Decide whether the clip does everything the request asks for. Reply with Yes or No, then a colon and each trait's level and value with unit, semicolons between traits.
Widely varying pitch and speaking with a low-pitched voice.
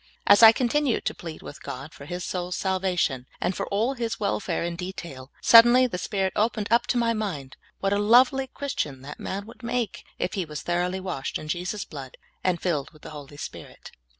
No: wide, 6.2 semitones; medium, 185 Hz